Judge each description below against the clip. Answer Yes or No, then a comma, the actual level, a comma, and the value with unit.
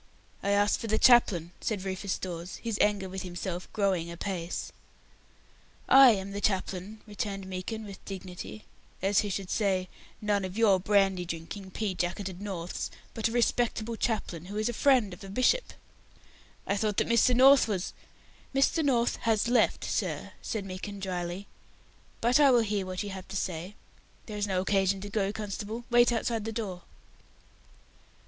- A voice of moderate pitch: No, high, 200 Hz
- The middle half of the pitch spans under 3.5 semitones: Yes, average, 2.9 semitones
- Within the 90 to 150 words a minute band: No, average, 170 wpm